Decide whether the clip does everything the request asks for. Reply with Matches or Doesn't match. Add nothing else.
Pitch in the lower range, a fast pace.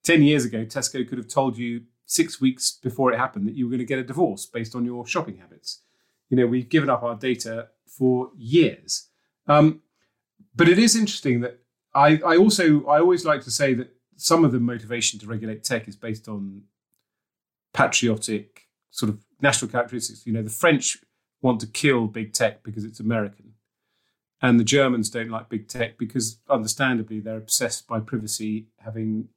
Doesn't match